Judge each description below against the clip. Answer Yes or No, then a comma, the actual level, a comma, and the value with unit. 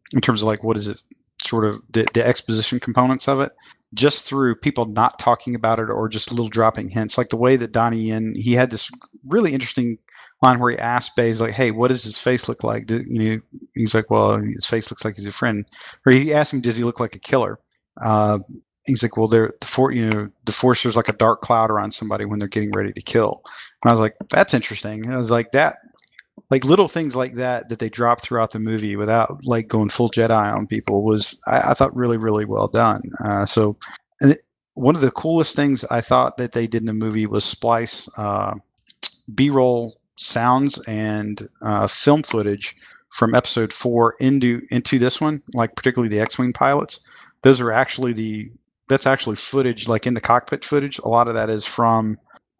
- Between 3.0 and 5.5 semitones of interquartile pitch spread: No, narrow, 2.4 semitones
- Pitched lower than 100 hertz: No, low, 115 Hz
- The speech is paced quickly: Yes, fast, 220 wpm